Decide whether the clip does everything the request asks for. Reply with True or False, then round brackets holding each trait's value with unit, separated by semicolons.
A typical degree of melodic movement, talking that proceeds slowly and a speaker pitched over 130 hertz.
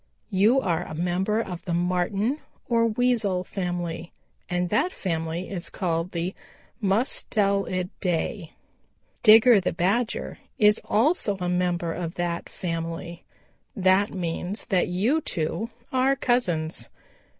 True (3.8 semitones; 130 wpm; 185 Hz)